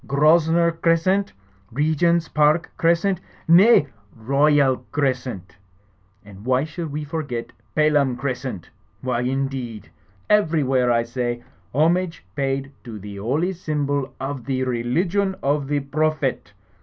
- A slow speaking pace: Yes, slow, 115 wpm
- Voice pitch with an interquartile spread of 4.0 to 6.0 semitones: Yes, average, 4.3 semitones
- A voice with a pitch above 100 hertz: Yes, medium, 140 Hz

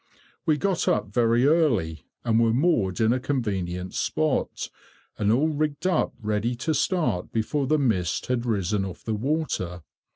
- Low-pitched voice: Yes, low, 115 Hz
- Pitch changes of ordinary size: No, wide, 6.9 semitones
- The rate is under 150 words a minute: No, average, 160 wpm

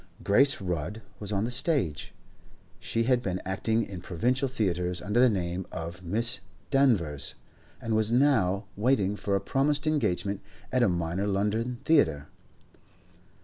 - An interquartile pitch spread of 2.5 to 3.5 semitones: No, wide, 5.5 semitones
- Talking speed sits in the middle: Yes, average, 145 wpm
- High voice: No, low, 105 Hz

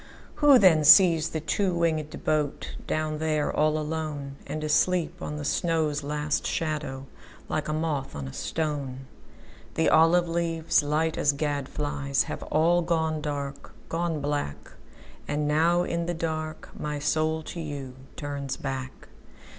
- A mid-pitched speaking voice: Yes, medium, 155 Hz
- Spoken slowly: Yes, slow, 125 wpm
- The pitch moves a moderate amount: No, narrow, 2.0 semitones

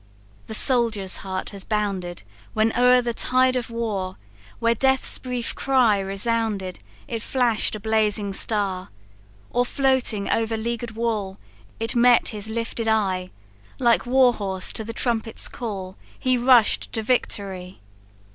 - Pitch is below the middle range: No, high, 225 Hz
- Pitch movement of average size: Yes, average, 3.3 semitones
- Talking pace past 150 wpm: No, slow, 135 wpm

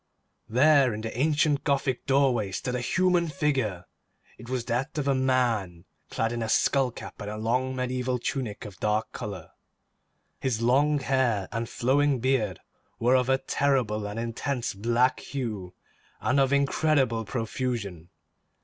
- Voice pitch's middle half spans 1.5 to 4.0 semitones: Yes, average, 3.4 semitones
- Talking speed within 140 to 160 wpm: Yes, average, 150 wpm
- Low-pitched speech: Yes, low, 125 Hz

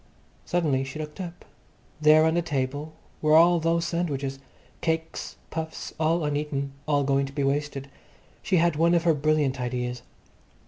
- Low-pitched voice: No, medium, 150 Hz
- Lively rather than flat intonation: No, average, 3.0 semitones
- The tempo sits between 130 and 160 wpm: Yes, average, 155 wpm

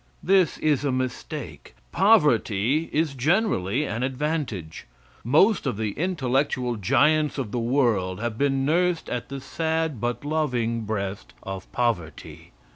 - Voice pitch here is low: Yes, low, 130 Hz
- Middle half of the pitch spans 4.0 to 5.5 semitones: Yes, average, 5.2 semitones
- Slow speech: Yes, slow, 130 wpm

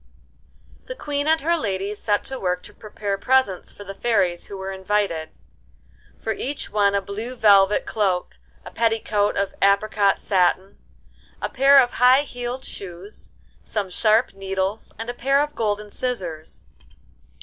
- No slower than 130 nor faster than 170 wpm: Yes, average, 150 wpm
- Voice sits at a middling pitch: No, high, 205 Hz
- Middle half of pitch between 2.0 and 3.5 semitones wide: No, average, 4.0 semitones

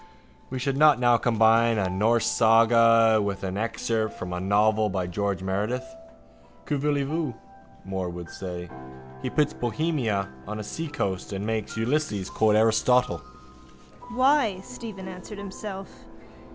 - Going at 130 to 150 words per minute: Yes, average, 140 wpm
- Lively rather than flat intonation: Yes, wide, 6.6 semitones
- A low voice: Yes, low, 110 Hz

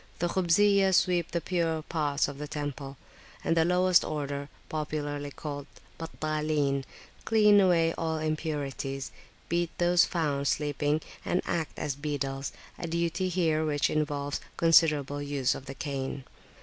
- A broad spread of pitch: No, average, 2.9 semitones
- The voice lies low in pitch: No, medium, 155 Hz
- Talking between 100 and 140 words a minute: Yes, slow, 135 wpm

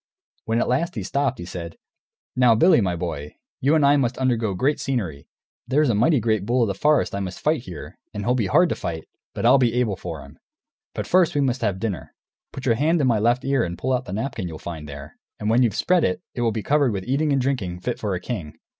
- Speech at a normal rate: No, fast, 255 wpm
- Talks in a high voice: No, low, 115 Hz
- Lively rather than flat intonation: Yes, wide, 6.3 semitones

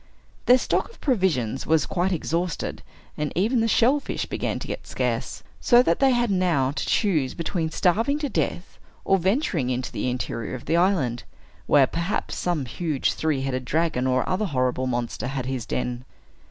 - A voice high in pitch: No, medium, 165 Hz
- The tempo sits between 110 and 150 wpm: No, average, 175 wpm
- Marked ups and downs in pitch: Yes, wide, 7.0 semitones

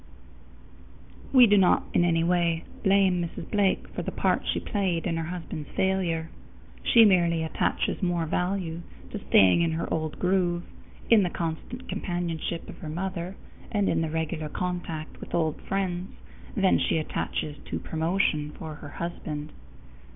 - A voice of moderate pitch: Yes, medium, 170 Hz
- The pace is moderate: Yes, average, 155 wpm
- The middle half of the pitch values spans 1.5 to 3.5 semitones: Yes, average, 2.7 semitones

